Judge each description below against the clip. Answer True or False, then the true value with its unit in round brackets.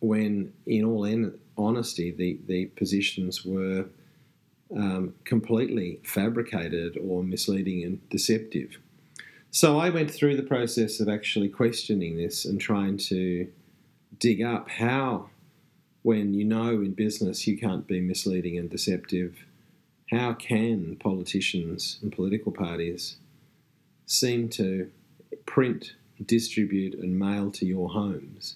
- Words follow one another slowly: True (120 wpm)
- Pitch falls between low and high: False (105 Hz)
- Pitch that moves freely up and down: False (3.7 semitones)